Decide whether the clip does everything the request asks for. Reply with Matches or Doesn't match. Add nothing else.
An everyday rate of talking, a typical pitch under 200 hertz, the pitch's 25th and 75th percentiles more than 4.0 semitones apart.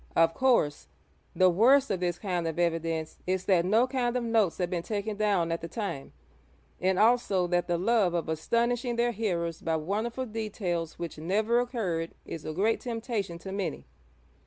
Matches